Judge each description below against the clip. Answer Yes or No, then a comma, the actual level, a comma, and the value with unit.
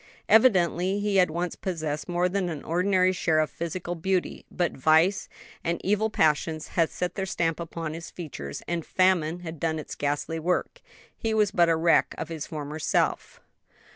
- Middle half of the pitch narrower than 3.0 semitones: Yes, narrow, 2.6 semitones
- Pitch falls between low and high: Yes, medium, 170 Hz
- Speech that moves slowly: No, average, 175 wpm